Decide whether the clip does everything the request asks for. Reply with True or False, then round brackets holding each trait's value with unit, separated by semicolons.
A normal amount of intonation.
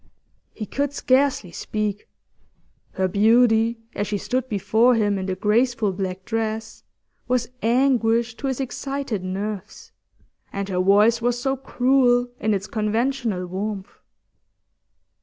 True (3.5 semitones)